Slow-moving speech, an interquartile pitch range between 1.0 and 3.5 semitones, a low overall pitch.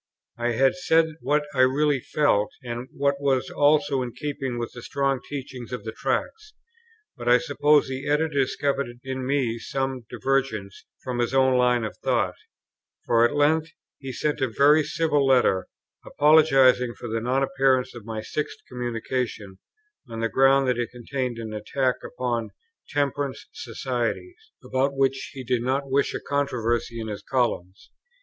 No: average, 160 wpm; average, 2.8 semitones; low, 130 Hz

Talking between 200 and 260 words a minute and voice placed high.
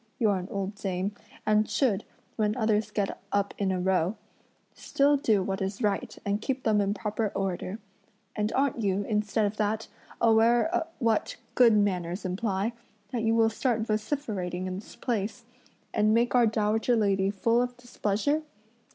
No: average, 160 wpm; high, 215 Hz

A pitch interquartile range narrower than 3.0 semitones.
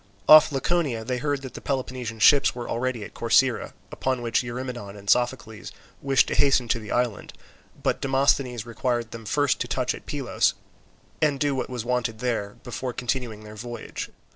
Yes: narrow, 2.5 semitones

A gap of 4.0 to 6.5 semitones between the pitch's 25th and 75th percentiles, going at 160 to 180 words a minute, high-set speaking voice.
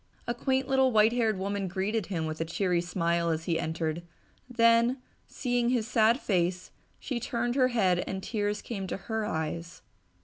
Yes: wide, 5.5 semitones; average, 175 wpm; high, 205 Hz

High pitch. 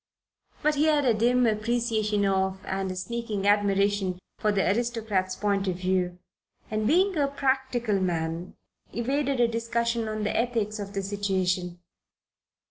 Yes: high, 210 Hz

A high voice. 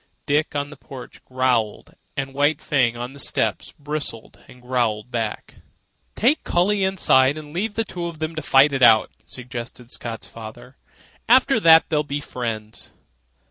No: medium, 140 Hz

